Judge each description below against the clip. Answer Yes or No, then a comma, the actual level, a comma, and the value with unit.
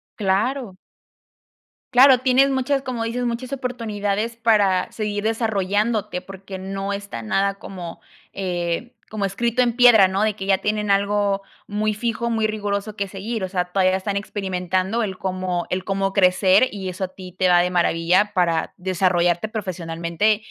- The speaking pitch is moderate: No, high, 200 Hz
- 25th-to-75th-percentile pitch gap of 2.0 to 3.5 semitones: Yes, average, 2.9 semitones